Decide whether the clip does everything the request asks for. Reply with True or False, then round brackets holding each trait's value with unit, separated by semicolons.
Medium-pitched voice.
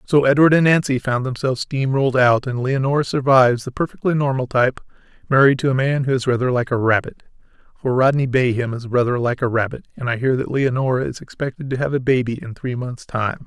False (130 Hz)